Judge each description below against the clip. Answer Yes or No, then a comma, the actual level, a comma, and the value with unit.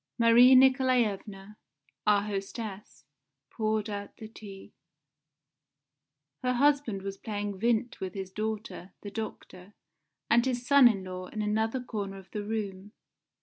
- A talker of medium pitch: No, high, 210 Hz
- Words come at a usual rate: No, slow, 130 wpm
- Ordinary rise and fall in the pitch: Yes, average, 3.2 semitones